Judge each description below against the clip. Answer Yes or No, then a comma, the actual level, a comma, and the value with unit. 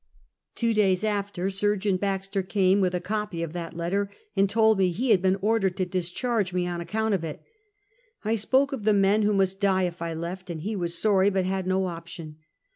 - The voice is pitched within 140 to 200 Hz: Yes, high, 190 Hz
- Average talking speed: No, fast, 215 wpm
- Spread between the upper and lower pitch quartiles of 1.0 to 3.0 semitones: Yes, narrow, 2.6 semitones